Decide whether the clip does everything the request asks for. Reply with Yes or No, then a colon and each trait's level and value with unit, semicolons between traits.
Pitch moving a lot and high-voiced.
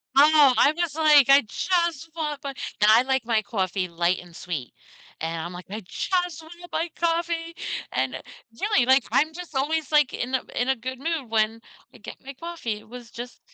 Yes: wide, 6.4 semitones; very high, 270 Hz